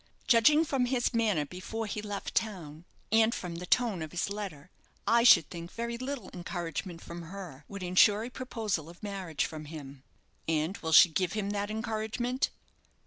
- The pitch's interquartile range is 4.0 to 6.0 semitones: Yes, average, 5.1 semitones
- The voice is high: Yes, high, 200 Hz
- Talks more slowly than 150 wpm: No, average, 175 wpm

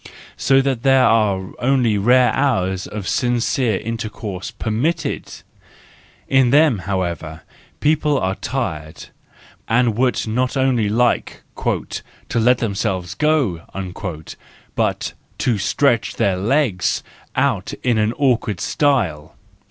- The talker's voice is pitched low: Yes, low, 115 Hz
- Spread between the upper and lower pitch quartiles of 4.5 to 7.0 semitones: Yes, average, 5.2 semitones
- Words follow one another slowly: Yes, slow, 115 wpm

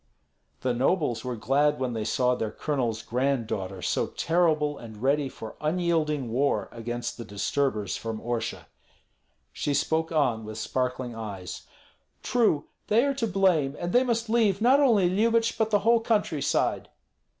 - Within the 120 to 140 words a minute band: No, average, 155 wpm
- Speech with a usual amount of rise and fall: No, wide, 8.2 semitones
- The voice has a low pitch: No, medium, 145 Hz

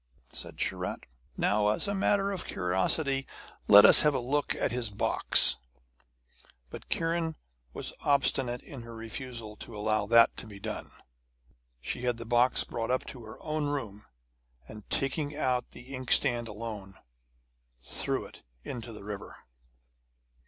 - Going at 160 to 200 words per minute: No, average, 145 wpm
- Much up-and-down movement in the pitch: No, average, 4.3 semitones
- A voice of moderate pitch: No, low, 120 Hz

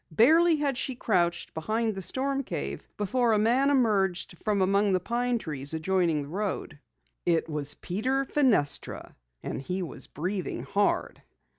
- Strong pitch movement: Yes, wide, 6.3 semitones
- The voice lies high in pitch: Yes, high, 200 Hz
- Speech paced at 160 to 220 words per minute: No, average, 150 wpm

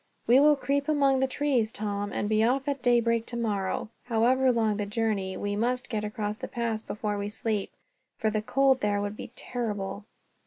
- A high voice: Yes, high, 225 Hz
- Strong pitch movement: No, average, 3.4 semitones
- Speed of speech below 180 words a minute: No, average, 190 wpm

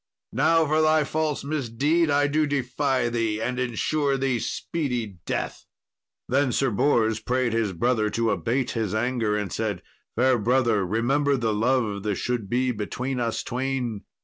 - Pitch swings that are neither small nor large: Yes, average, 3.7 semitones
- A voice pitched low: Yes, low, 125 Hz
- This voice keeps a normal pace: Yes, average, 155 wpm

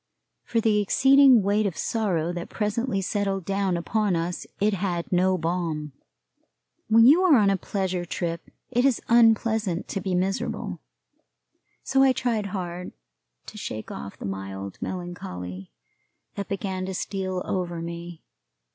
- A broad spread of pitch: No, average, 3.7 semitones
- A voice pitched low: No, high, 190 Hz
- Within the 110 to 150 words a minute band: Yes, average, 145 wpm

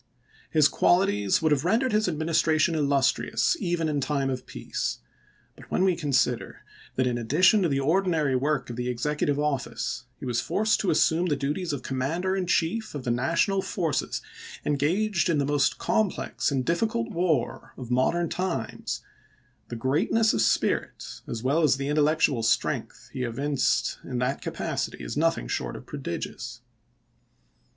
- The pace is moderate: Yes, average, 160 wpm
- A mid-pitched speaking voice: Yes, medium, 150 Hz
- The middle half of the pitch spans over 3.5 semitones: Yes, average, 5.0 semitones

